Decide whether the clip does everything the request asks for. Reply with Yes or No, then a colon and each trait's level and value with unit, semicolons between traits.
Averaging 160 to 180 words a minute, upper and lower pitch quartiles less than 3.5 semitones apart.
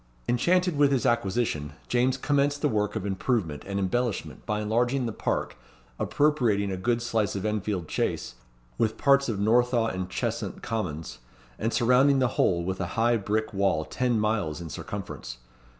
No: average, 165 wpm; average, 4.3 semitones